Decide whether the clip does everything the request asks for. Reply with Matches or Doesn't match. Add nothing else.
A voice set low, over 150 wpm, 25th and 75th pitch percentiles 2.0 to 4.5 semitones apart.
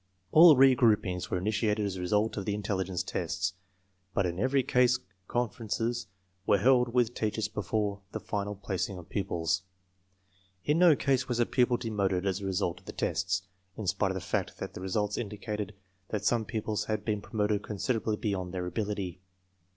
Matches